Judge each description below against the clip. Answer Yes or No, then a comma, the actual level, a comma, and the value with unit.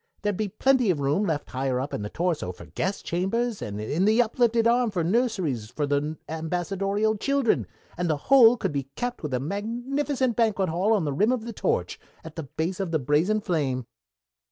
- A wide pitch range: Yes, wide, 7.3 semitones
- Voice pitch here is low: No, medium, 185 Hz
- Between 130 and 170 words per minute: No, fast, 205 wpm